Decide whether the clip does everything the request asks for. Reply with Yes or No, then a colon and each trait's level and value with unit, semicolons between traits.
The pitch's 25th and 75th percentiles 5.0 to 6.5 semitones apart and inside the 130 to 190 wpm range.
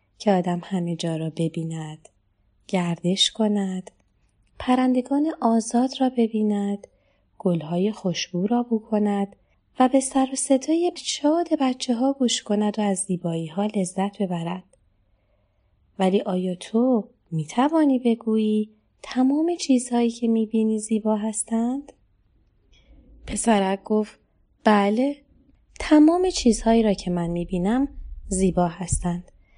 No: wide, 5.6 semitones; average, 115 wpm